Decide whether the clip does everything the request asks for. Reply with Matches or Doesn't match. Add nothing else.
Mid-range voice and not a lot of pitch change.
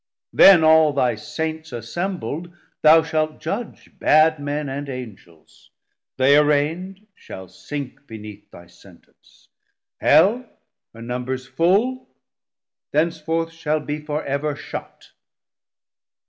Doesn't match